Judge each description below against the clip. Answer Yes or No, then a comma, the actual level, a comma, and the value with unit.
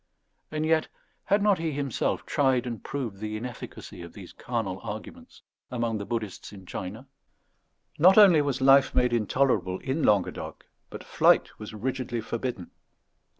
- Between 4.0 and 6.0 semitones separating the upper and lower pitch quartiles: Yes, average, 4.7 semitones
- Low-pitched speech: Yes, low, 120 Hz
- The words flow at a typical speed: Yes, average, 150 wpm